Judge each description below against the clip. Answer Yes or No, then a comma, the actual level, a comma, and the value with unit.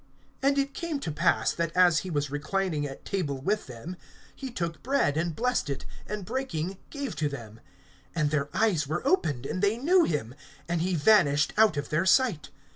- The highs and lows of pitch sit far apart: Yes, wide, 7.1 semitones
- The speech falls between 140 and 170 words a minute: No, average, 195 wpm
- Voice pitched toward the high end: No, medium, 175 Hz